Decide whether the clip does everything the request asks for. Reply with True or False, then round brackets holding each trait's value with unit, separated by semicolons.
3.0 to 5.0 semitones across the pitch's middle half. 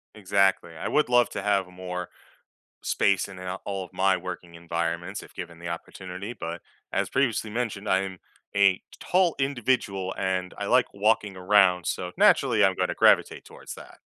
False (2.5 semitones)